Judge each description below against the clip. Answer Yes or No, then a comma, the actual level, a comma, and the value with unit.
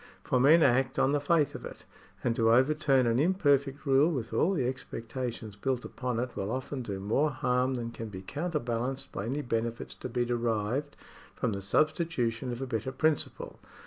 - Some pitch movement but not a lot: Yes, average, 3.5 semitones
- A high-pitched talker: No, low, 130 Hz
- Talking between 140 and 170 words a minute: No, average, 185 wpm